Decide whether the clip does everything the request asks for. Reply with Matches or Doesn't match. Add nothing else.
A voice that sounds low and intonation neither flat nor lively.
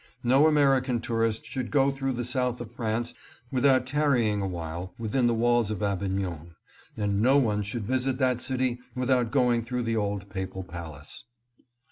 Matches